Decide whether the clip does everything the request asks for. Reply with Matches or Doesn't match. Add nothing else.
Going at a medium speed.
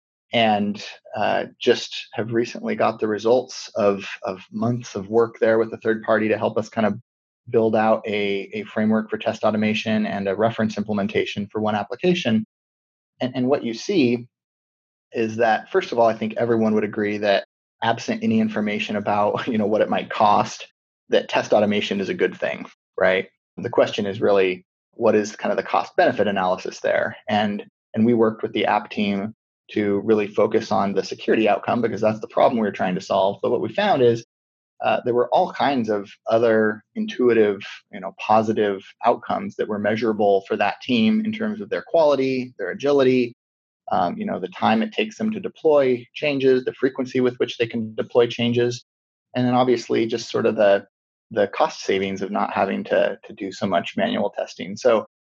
Matches